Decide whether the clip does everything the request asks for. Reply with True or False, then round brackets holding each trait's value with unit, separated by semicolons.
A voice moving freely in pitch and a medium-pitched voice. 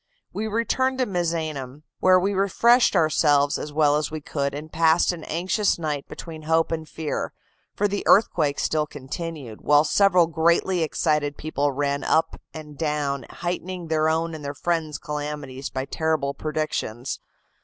False (2.7 semitones; 155 Hz)